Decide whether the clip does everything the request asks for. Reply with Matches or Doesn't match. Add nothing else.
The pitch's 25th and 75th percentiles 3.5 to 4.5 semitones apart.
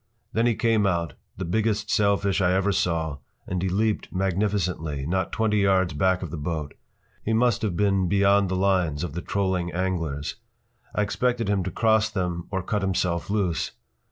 Doesn't match